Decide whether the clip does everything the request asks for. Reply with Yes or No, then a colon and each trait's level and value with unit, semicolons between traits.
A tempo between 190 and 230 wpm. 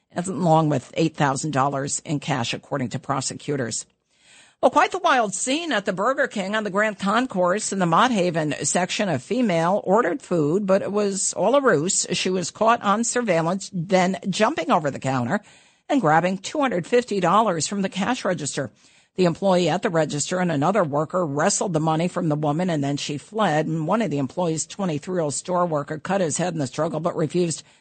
Yes: fast, 205 wpm